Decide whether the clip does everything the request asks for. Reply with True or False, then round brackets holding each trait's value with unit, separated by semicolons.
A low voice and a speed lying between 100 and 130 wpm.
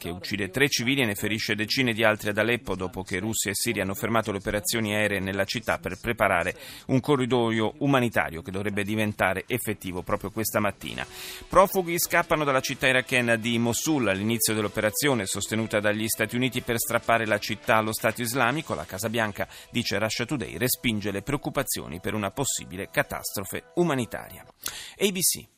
False (110 Hz; 165 wpm)